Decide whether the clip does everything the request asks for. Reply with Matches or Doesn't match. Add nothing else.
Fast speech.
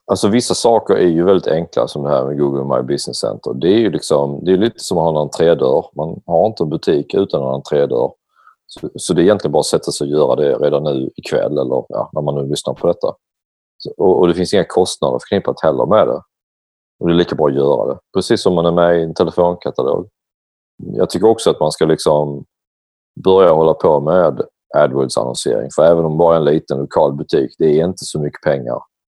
Matches